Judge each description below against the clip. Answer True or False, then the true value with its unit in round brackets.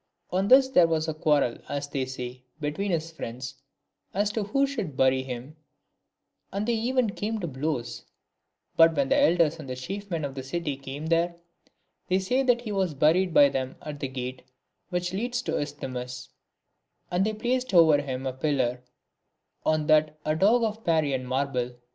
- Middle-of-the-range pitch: True (155 Hz)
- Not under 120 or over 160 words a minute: False (185 wpm)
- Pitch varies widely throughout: True (6.6 semitones)